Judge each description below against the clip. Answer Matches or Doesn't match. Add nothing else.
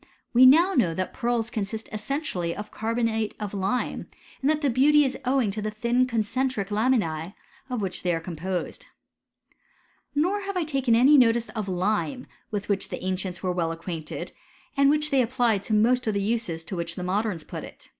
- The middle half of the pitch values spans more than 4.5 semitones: Matches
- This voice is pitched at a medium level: Doesn't match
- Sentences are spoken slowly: Doesn't match